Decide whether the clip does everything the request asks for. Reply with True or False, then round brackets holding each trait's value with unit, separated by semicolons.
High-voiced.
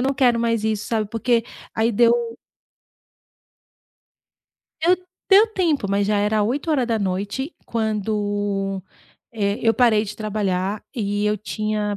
True (215 Hz)